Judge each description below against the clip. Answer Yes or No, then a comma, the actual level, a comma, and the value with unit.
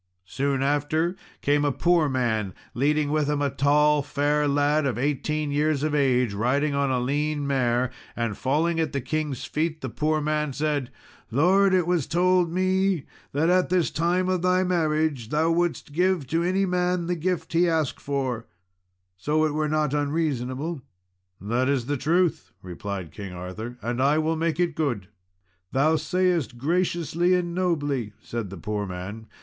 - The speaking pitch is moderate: Yes, medium, 150 Hz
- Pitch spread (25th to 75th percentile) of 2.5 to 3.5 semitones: No, average, 4.2 semitones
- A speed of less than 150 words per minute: No, average, 170 wpm